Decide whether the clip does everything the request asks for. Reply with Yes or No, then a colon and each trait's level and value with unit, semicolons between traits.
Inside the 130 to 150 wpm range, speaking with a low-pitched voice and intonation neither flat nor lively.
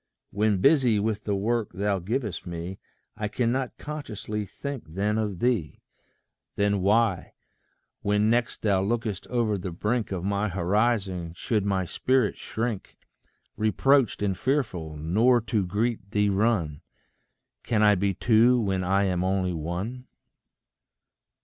Yes: slow, 135 wpm; low, 105 Hz; average, 3.6 semitones